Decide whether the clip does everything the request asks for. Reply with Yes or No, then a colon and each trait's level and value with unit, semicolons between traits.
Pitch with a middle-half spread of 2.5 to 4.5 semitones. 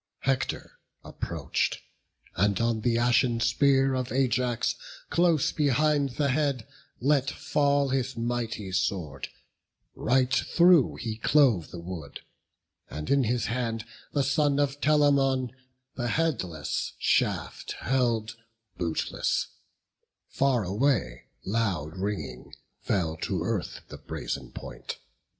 No: average, 5.0 semitones